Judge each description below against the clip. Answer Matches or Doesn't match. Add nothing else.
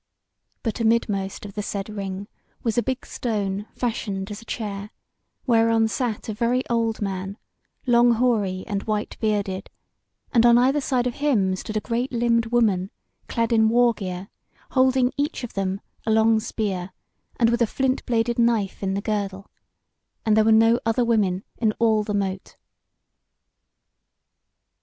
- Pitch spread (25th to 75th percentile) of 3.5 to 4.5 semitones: Doesn't match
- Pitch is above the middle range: Matches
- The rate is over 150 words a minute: Matches